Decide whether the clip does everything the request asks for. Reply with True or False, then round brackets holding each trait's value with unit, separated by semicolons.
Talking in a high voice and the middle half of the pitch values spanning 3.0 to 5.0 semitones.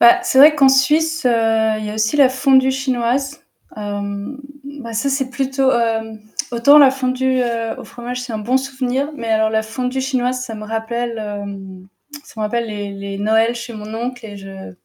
True (240 Hz; 3.4 semitones)